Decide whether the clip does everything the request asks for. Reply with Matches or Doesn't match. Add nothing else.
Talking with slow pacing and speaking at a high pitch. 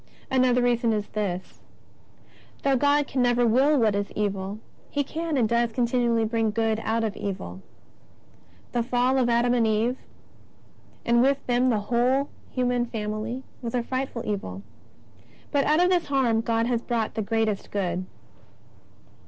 Doesn't match